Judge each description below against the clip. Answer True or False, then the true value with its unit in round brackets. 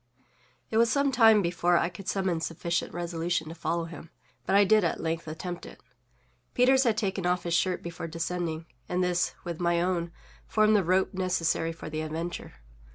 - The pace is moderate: True (185 wpm)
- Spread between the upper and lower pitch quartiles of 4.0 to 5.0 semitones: False (2.4 semitones)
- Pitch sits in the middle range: True (175 Hz)